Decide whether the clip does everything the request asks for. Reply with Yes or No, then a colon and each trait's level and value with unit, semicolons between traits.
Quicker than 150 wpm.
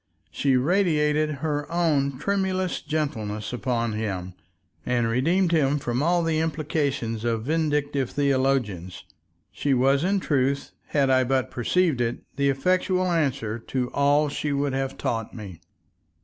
No: slow, 135 wpm